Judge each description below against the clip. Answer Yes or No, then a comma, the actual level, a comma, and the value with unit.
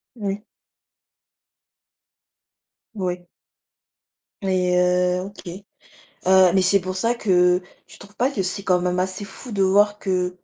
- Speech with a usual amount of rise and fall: No, narrow, 1.8 semitones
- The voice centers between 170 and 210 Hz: Yes, high, 190 Hz